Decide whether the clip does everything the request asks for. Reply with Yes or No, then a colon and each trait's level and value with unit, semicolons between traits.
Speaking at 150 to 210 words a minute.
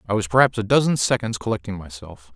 Yes: fast, 205 wpm